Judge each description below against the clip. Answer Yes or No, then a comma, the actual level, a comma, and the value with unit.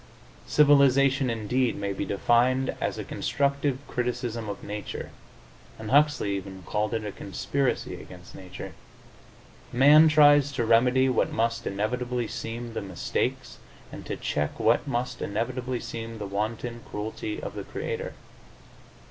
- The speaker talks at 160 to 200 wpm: No, slow, 135 wpm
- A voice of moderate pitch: No, low, 120 Hz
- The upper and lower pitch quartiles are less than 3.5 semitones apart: No, average, 4.0 semitones